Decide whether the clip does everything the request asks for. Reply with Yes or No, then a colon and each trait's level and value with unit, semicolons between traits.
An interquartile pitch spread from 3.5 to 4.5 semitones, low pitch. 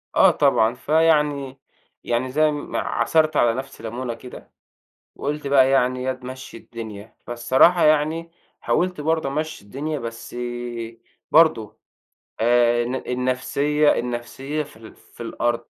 Yes: average, 3.9 semitones; low, 130 Hz